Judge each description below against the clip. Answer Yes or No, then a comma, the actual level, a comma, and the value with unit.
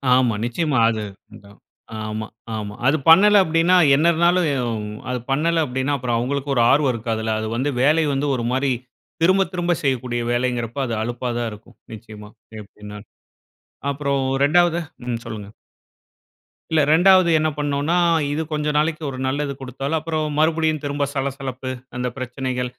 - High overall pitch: No, low, 135 Hz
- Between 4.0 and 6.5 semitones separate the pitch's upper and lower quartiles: Yes, average, 4.6 semitones